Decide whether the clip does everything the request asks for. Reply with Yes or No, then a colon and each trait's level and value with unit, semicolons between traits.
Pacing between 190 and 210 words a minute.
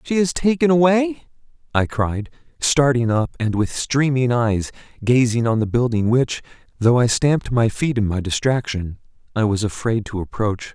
No: average, 170 wpm